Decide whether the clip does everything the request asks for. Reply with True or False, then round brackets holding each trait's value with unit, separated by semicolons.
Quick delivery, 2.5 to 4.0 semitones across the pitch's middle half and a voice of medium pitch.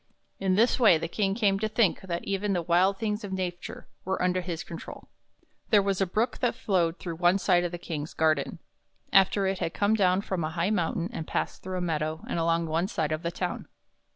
True (225 wpm; 2.8 semitones; 180 Hz)